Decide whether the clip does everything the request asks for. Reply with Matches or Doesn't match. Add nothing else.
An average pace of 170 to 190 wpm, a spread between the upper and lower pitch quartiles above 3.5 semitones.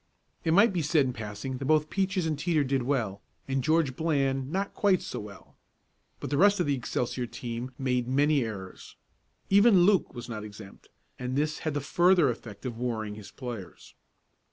Matches